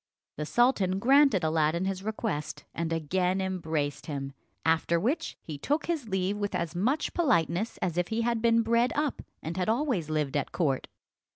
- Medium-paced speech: Yes, average, 175 wpm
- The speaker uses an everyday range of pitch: No, wide, 6.3 semitones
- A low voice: No, medium, 185 Hz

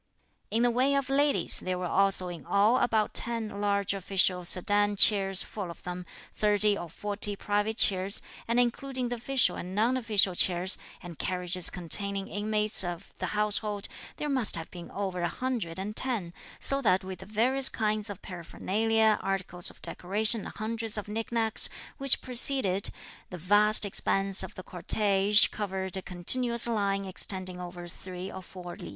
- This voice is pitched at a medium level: No, high, 205 Hz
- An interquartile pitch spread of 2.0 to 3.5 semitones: Yes, average, 3.2 semitones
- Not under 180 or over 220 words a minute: No, average, 170 wpm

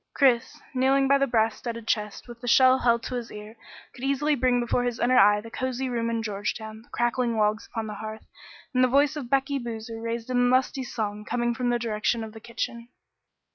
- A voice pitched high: Yes, high, 235 Hz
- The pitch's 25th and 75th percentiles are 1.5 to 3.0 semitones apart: Yes, narrow, 2.4 semitones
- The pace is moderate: No, fast, 215 wpm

